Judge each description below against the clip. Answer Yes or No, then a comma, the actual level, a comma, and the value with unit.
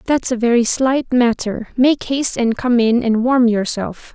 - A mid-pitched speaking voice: No, high, 240 Hz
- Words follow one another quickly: No, average, 190 wpm